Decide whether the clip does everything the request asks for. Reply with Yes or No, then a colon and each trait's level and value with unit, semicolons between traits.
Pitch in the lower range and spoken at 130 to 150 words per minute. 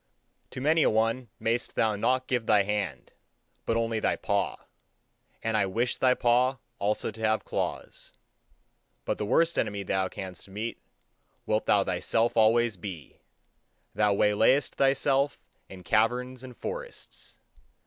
Yes: low, 115 Hz; average, 140 wpm